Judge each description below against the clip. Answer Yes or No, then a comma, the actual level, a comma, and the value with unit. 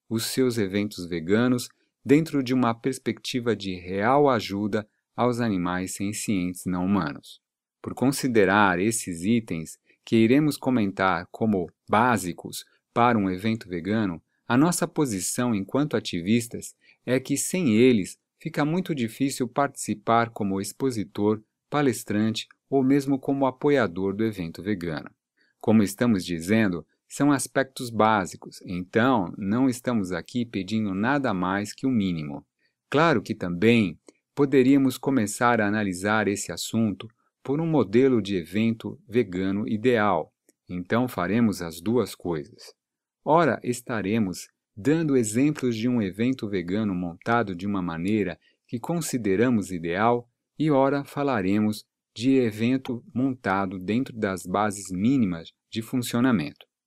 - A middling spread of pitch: Yes, average, 4.8 semitones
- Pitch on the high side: No, low, 110 Hz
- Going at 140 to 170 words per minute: No, average, 125 wpm